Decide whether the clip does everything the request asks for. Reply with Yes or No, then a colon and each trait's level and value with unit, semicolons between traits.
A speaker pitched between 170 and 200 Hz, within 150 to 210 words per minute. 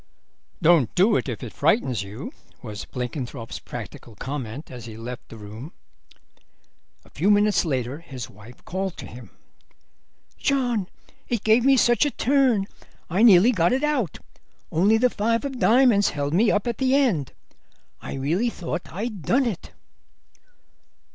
Yes: medium, 185 Hz; average, 155 wpm